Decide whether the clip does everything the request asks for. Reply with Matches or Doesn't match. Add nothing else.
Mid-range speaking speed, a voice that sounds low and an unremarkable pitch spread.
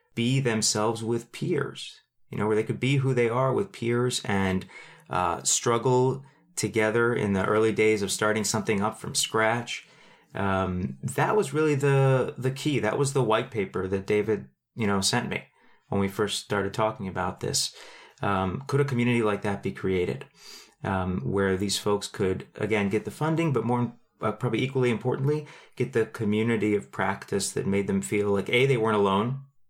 Matches